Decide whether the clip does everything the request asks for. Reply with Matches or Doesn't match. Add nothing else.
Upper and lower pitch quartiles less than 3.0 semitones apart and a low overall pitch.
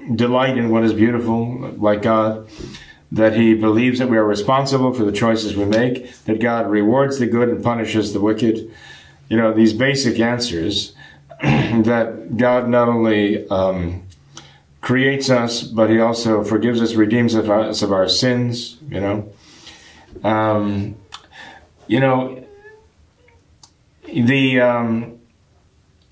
Matches